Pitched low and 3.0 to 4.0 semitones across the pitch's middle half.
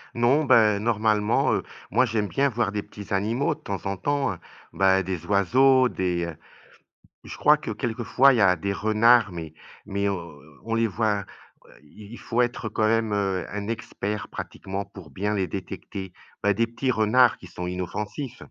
Yes: low, 105 Hz; average, 3.3 semitones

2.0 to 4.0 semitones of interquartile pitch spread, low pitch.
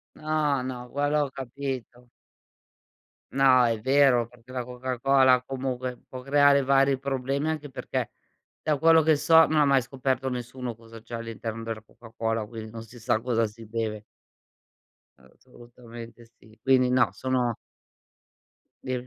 Yes: average, 2.9 semitones; low, 125 Hz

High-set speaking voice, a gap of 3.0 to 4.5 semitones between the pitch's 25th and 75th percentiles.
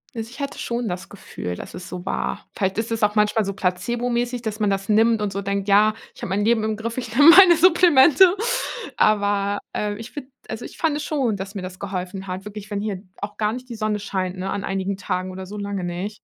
Yes: high, 210 Hz; average, 3.3 semitones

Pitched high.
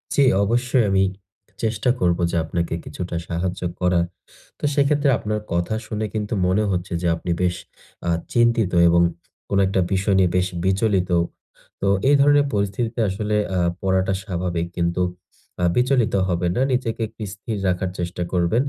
No: very low, 95 Hz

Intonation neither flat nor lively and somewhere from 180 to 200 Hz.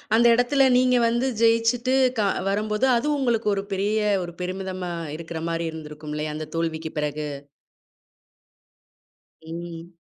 No: wide, 6.0 semitones; high, 190 Hz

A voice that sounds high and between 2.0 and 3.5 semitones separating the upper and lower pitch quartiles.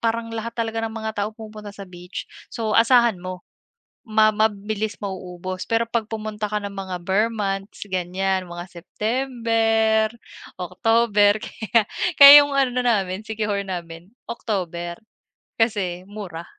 Yes: high, 210 Hz; average, 3.2 semitones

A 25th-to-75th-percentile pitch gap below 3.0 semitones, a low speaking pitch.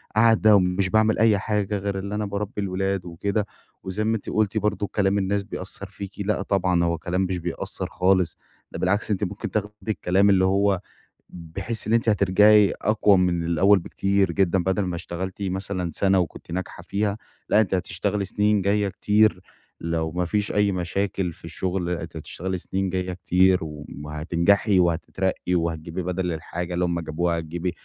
Yes: narrow, 2.5 semitones; very low, 95 Hz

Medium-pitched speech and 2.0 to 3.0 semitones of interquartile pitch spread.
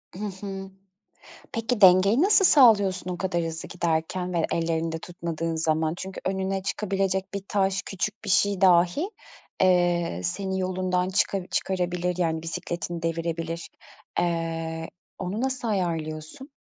Yes: medium, 180 Hz; narrow, 2.6 semitones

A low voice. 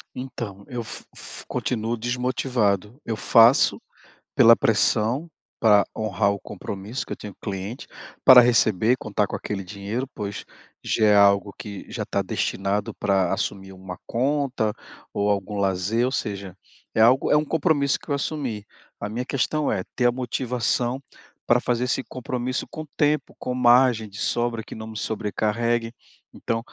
Yes: low, 115 Hz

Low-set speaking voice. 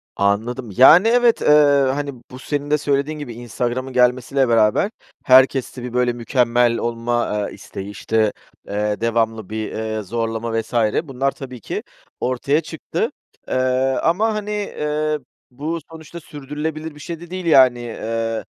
Yes: low, 130 Hz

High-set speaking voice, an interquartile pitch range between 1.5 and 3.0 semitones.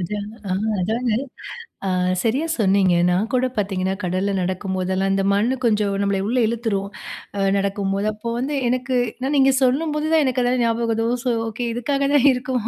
No: high, 225 Hz; average, 4.4 semitones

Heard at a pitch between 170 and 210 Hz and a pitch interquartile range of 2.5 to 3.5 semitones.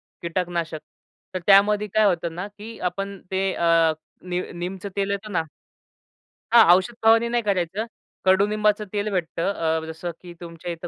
Yes: high, 190 Hz; average, 3.2 semitones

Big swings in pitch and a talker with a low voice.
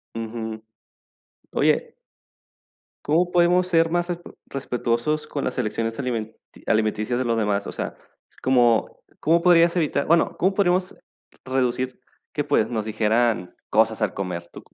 Yes: wide, 7.1 semitones; low, 125 Hz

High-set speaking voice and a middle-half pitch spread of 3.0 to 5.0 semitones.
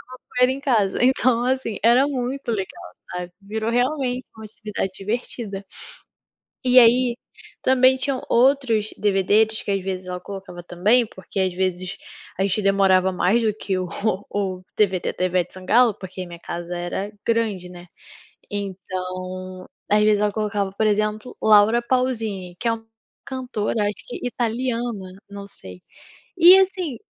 Yes: high, 210 Hz; average, 4.4 semitones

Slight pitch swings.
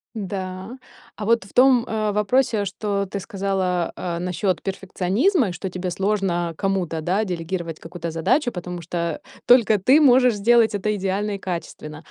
No: average, 3.3 semitones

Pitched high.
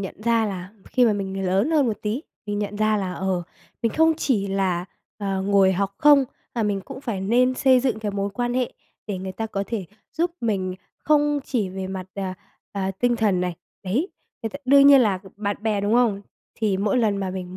Yes: high, 205 Hz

